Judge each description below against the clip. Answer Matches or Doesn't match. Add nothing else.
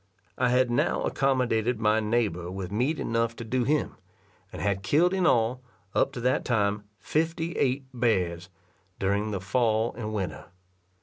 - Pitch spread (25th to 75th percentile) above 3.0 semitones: Matches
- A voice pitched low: Matches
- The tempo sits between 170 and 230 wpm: Doesn't match